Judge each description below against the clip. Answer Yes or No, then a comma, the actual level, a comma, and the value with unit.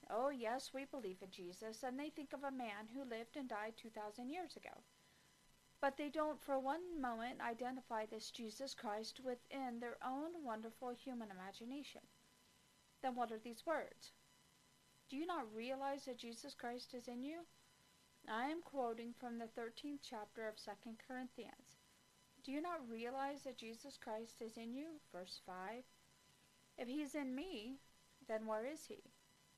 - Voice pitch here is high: Yes, very high, 250 Hz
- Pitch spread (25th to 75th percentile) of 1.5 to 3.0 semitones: No, average, 3.5 semitones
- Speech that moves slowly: No, average, 165 wpm